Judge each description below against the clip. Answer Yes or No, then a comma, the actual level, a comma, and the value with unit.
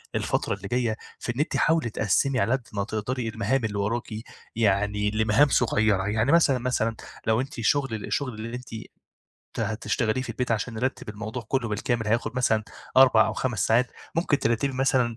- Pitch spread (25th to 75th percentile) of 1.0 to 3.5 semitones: Yes, average, 2.9 semitones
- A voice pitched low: Yes, low, 115 Hz